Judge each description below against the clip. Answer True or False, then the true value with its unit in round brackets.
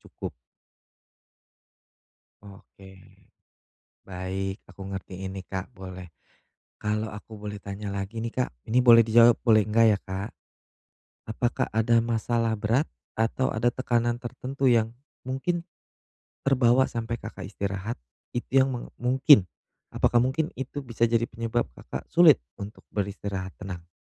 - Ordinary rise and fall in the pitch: True (3.5 semitones)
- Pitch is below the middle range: True (115 Hz)